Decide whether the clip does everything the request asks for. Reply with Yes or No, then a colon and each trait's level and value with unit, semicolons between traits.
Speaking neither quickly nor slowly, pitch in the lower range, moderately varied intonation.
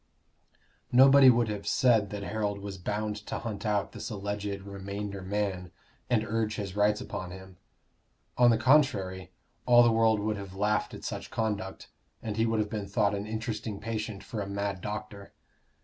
No: average, 175 wpm; low, 105 Hz; narrow, 2.0 semitones